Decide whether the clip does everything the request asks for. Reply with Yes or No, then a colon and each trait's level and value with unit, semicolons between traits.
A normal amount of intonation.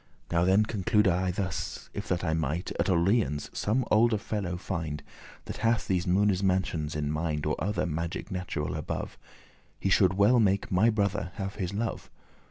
Yes: average, 3.4 semitones